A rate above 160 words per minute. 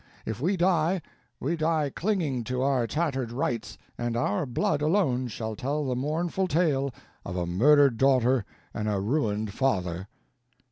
No: average, 150 wpm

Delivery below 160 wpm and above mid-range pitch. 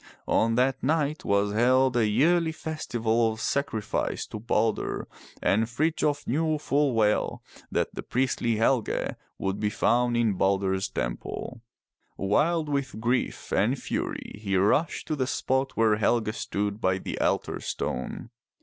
No: average, 150 wpm; low, 115 Hz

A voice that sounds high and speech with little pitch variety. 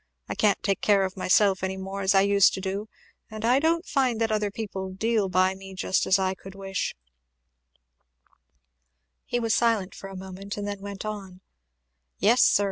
Yes: high, 195 Hz; narrow, 2.0 semitones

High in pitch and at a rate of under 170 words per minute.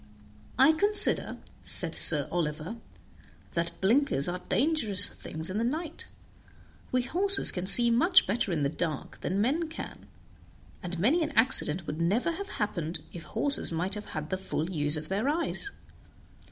Yes: high, 200 Hz; average, 160 wpm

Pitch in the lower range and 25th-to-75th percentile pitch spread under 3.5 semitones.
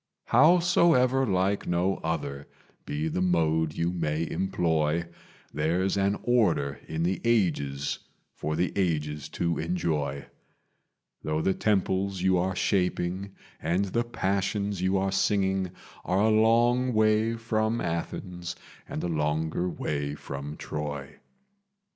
No: very low, 90 Hz; average, 4.2 semitones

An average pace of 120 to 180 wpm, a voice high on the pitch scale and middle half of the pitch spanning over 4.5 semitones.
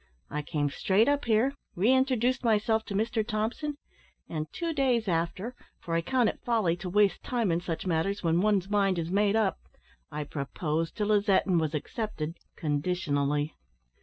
Yes: average, 170 wpm; high, 195 Hz; average, 5.3 semitones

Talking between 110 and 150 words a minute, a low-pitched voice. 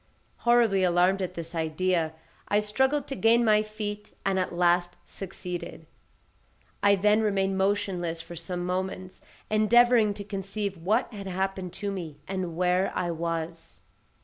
No: average, 145 wpm; high, 190 Hz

